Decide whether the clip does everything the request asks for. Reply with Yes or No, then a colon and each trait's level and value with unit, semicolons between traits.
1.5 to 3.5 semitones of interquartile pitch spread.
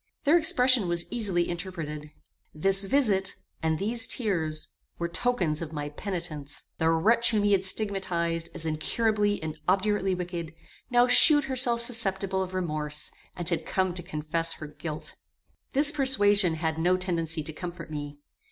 No: average, 4.6 semitones